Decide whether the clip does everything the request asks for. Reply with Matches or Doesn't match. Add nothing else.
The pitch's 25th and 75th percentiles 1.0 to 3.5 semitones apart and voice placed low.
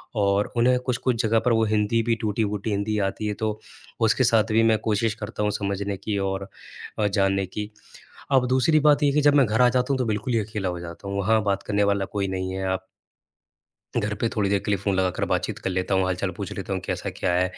Matches